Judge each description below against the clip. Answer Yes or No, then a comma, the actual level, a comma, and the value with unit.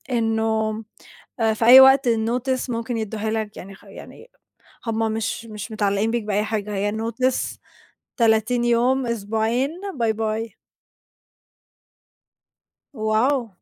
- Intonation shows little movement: Yes, narrow, 1.7 semitones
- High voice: Yes, high, 225 Hz